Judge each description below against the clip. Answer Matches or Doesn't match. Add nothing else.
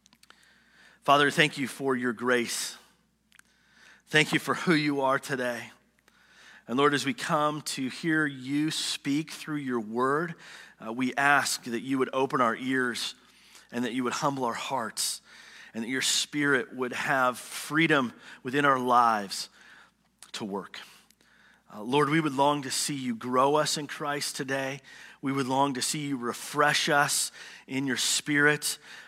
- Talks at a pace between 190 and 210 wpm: Doesn't match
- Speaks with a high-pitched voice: Doesn't match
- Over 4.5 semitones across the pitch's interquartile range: Doesn't match